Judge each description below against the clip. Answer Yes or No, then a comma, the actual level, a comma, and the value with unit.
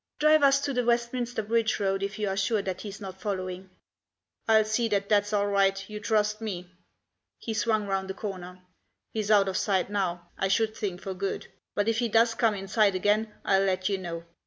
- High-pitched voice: Yes, high, 205 Hz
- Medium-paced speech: No, fast, 215 wpm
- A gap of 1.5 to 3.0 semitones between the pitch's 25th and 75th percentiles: Yes, narrow, 2.5 semitones